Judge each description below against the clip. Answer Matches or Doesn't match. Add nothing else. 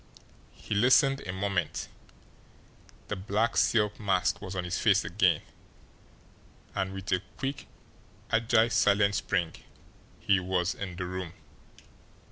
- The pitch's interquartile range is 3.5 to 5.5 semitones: Doesn't match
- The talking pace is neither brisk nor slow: Doesn't match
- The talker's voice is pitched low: Matches